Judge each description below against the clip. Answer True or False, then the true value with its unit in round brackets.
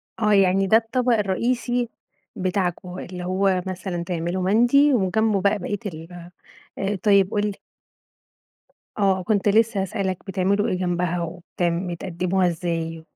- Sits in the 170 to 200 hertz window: True (190 Hz)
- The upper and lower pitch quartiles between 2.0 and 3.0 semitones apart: True (2.7 semitones)